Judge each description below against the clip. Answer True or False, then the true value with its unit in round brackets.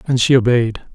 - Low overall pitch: True (120 Hz)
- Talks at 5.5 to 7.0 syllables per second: True (5.6 syllables/s)